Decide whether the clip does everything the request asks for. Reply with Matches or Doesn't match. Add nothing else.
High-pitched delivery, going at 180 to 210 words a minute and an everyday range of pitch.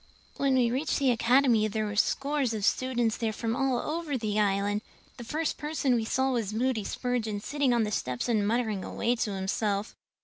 Matches